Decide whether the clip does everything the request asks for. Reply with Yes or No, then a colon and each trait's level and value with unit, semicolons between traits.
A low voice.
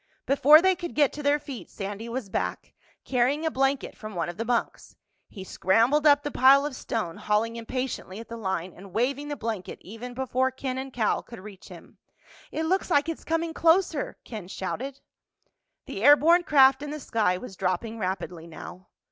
No: very high, 250 Hz